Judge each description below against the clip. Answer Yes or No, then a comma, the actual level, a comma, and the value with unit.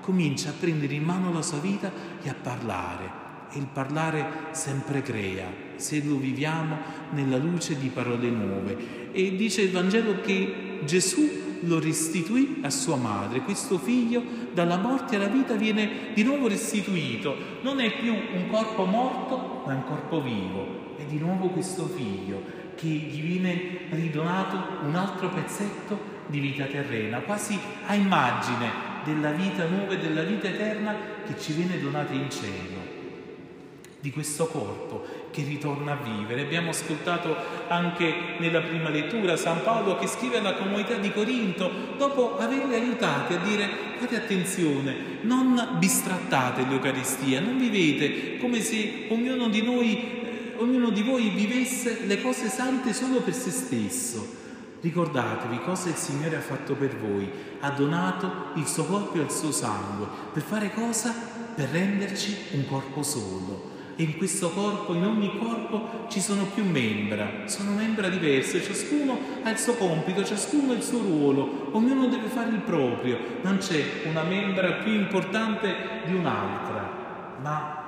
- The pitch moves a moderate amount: No, wide, 6.4 semitones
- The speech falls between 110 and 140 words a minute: No, average, 155 wpm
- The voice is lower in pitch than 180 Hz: No, medium, 185 Hz